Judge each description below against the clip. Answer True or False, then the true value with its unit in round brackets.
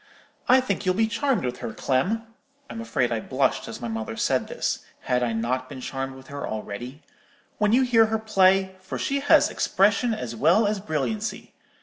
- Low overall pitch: False (185 Hz)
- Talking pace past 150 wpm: True (185 wpm)